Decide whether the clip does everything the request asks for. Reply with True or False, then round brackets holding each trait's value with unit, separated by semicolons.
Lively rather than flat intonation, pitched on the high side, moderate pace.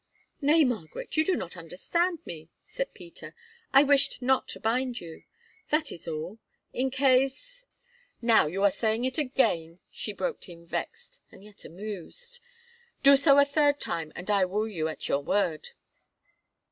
True (8.4 semitones; 245 Hz; 165 wpm)